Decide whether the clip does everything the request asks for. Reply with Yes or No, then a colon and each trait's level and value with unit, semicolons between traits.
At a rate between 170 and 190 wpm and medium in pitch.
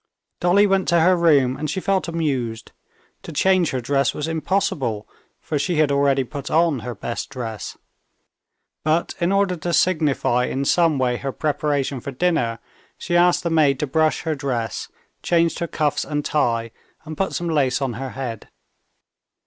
Yes: average, 175 wpm; medium, 150 Hz